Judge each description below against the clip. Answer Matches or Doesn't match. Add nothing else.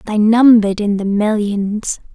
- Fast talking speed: Doesn't match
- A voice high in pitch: Matches